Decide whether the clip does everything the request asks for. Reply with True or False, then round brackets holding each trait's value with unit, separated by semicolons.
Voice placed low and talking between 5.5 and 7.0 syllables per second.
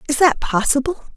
False (285 Hz; 5.7 syllables/s)